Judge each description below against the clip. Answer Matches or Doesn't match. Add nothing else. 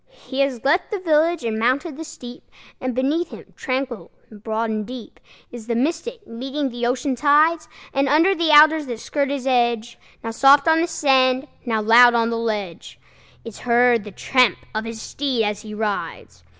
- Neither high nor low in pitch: Doesn't match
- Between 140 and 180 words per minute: Doesn't match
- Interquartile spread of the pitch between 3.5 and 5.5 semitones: Matches